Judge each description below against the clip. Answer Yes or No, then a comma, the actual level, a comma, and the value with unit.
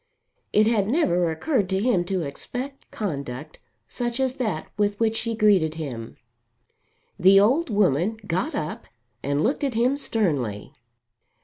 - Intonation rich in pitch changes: Yes, wide, 6.7 semitones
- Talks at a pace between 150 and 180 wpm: No, average, 140 wpm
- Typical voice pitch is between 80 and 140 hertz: No, high, 205 Hz